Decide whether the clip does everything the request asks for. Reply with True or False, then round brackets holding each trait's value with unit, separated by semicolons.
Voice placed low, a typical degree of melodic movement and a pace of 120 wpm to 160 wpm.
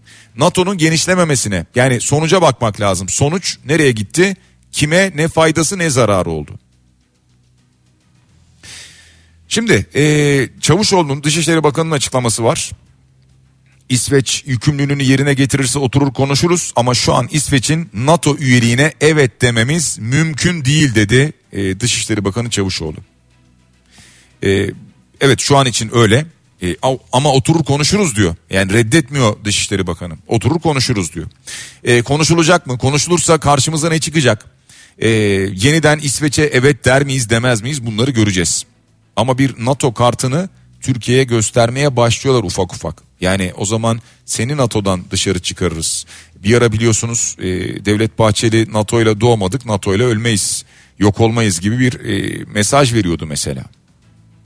False (120 Hz; 6.0 semitones; 125 wpm)